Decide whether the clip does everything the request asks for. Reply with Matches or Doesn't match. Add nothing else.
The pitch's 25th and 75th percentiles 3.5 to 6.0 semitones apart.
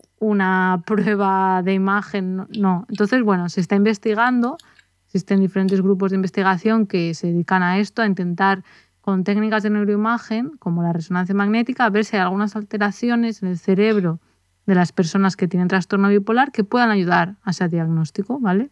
Doesn't match